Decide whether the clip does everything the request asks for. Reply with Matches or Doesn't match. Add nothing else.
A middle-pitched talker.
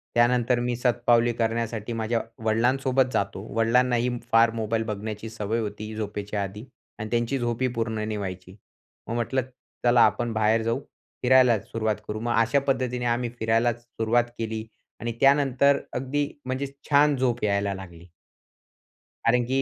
Doesn't match